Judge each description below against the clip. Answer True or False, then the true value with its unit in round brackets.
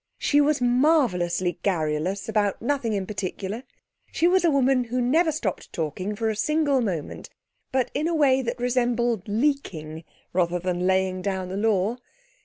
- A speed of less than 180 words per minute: True (160 wpm)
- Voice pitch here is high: True (220 Hz)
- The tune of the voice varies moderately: False (6.2 semitones)